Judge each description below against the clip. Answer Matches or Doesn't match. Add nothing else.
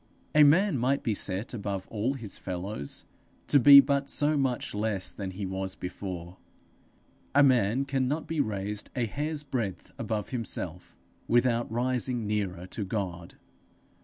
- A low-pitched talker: Matches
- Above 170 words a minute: Doesn't match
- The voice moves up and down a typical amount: Doesn't match